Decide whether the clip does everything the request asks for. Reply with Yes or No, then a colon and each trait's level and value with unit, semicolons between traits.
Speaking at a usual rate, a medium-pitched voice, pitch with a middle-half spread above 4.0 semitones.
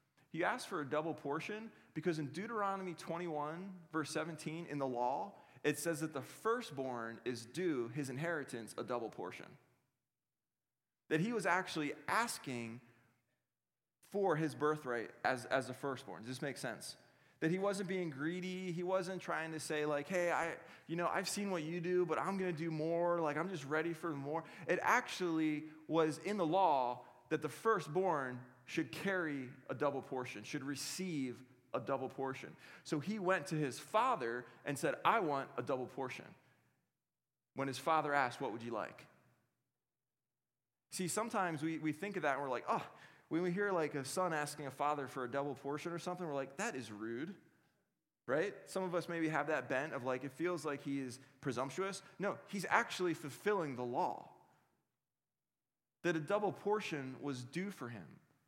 Yes: average, 180 wpm; medium, 155 Hz; average, 4.8 semitones